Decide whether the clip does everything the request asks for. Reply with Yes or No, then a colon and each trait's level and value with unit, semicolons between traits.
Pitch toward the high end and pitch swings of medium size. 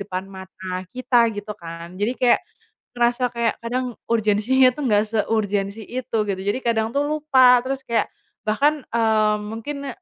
Yes: high, 230 Hz; average, 3.5 semitones